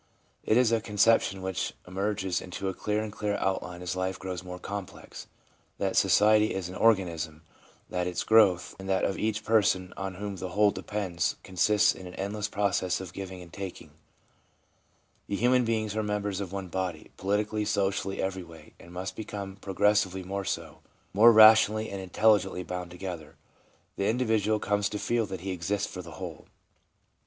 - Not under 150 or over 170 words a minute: No, average, 180 wpm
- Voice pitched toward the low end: Yes, low, 100 Hz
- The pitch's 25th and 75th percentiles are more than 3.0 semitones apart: No, narrow, 2.4 semitones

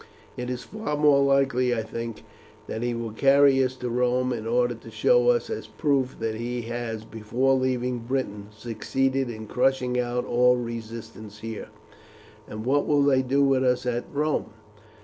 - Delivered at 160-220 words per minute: Yes, average, 170 wpm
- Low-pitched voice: Yes, low, 125 Hz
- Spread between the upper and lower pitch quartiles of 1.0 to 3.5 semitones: Yes, narrow, 2.5 semitones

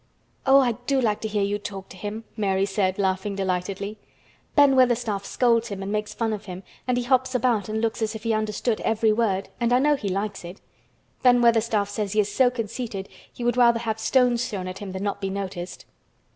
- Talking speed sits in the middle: No, fast, 220 wpm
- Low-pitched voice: No, high, 215 Hz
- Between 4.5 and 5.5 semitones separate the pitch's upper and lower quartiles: No, average, 3.2 semitones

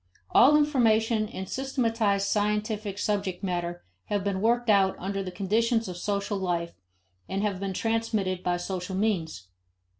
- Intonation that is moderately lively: Yes, average, 3.0 semitones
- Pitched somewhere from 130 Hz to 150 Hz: No, high, 200 Hz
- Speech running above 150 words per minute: No, average, 145 wpm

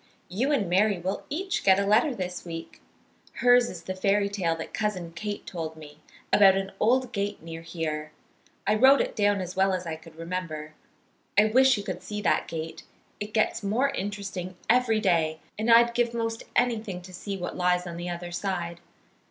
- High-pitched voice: Yes, high, 195 Hz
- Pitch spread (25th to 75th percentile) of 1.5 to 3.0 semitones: No, average, 3.9 semitones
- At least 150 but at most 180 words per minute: No, average, 195 wpm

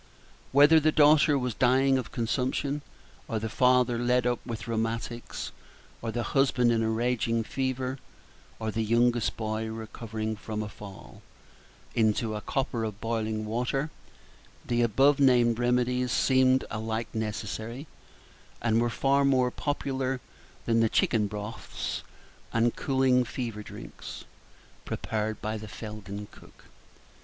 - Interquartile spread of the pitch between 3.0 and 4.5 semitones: No, narrow, 2.6 semitones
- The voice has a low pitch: Yes, low, 120 Hz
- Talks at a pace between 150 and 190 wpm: No, average, 140 wpm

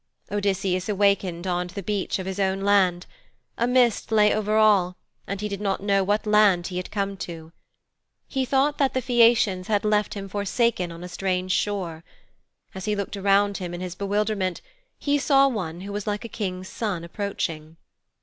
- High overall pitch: Yes, high, 200 Hz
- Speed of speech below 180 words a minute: No, average, 185 wpm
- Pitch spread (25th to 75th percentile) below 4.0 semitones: Yes, narrow, 2.5 semitones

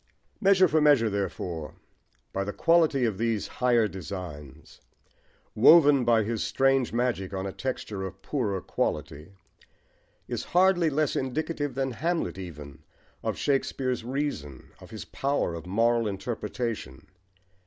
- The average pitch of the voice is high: No, low, 115 Hz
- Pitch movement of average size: No, wide, 6.5 semitones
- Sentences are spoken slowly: Yes, slow, 130 wpm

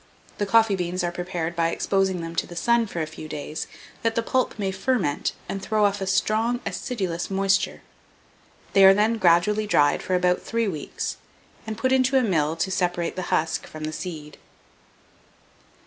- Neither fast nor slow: Yes, average, 180 wpm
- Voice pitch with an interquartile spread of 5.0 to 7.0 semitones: No, average, 4.1 semitones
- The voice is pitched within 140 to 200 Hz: Yes, high, 190 Hz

